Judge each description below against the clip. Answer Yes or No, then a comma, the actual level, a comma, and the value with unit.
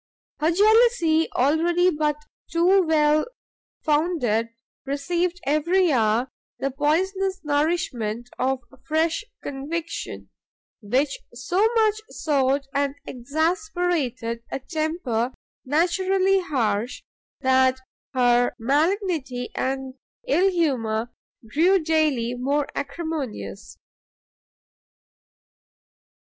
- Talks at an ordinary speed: No, slow, 80 wpm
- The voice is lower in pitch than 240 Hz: No, very high, 300 Hz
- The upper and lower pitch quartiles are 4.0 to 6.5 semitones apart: Yes, average, 5.2 semitones